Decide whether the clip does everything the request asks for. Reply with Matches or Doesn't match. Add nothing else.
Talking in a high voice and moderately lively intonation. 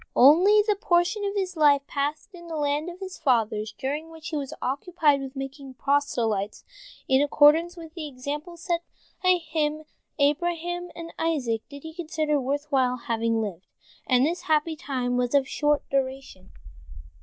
Matches